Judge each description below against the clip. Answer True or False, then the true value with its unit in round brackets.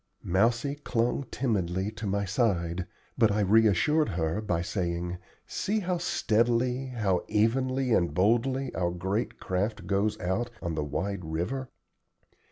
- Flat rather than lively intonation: False (5.2 semitones)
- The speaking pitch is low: True (105 Hz)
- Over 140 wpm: False (135 wpm)